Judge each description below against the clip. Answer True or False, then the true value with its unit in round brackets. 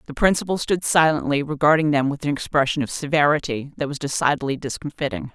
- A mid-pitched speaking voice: True (145 Hz)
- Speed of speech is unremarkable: True (170 wpm)